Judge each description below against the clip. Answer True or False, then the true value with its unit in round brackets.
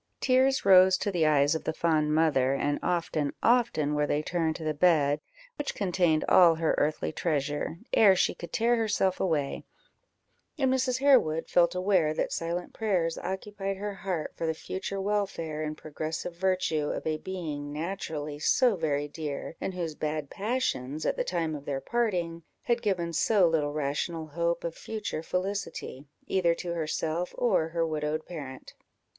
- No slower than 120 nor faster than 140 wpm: False (165 wpm)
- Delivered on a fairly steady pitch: False (3.8 semitones)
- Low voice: False (165 Hz)